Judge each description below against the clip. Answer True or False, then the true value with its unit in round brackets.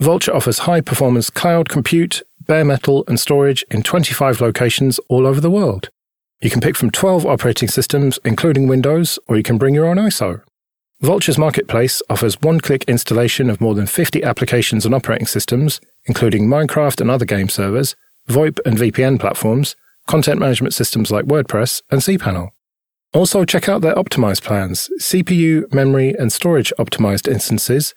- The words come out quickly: False (165 wpm)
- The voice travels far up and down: False (5.0 semitones)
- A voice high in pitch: False (135 Hz)